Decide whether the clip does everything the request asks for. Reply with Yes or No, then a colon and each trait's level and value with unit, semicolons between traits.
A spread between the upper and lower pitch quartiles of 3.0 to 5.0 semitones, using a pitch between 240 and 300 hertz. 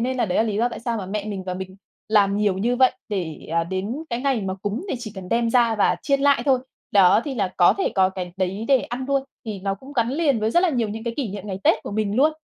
No: average, 4.4 semitones; high, 215 Hz